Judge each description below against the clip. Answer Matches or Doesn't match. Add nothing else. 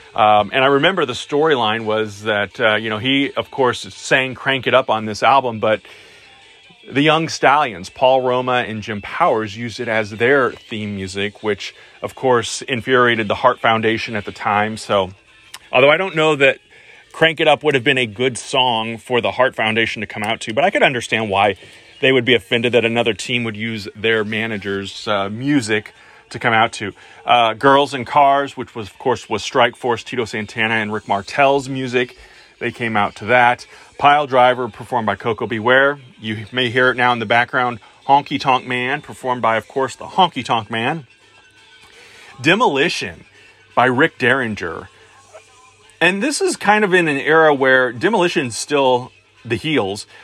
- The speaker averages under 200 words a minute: Matches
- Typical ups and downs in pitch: Matches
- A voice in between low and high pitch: Doesn't match